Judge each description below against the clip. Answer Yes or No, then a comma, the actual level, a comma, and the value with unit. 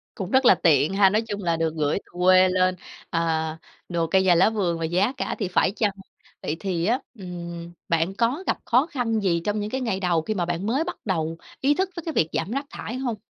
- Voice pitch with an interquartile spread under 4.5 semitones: No, average, 5.1 semitones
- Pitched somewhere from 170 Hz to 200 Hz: Yes, high, 190 Hz